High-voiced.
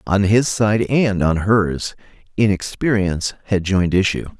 No: low, 100 Hz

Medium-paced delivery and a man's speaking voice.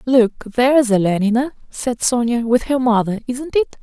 No: average, 155 wpm; female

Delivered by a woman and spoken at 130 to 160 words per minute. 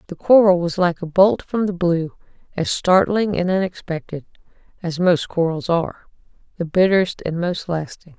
Yes: female; average, 145 wpm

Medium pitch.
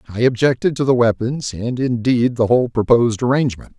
No: low, 120 Hz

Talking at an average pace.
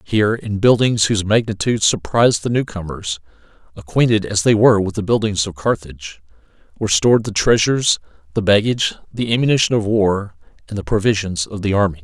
Yes: average, 165 wpm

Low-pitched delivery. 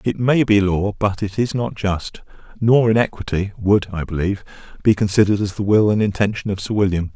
Yes: low, 100 Hz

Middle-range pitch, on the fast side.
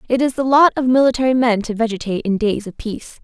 No: high, 240 Hz; fast, 240 wpm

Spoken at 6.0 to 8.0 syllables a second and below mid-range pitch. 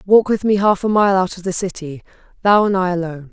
No: 6.2 syllables/s; high, 190 Hz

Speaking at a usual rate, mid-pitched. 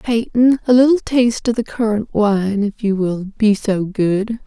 No: average, 175 wpm; high, 220 Hz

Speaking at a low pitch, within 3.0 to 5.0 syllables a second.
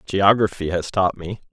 Yes: very low, 95 Hz; 4.7 syllables/s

